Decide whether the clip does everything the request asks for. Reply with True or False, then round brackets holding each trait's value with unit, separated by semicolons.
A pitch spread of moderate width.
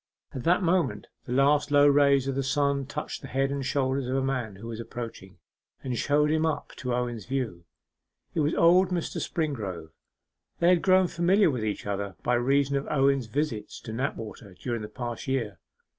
True (3.9 semitones)